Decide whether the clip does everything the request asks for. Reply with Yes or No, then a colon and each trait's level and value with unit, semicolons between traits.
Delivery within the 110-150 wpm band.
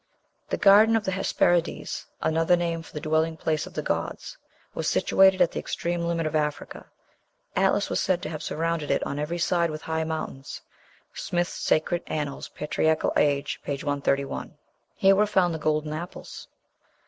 No: average, 170 wpm